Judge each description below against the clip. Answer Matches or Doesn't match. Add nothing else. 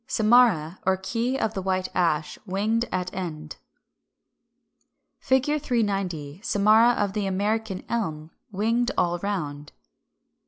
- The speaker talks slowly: Matches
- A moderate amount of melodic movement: Matches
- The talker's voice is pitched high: Matches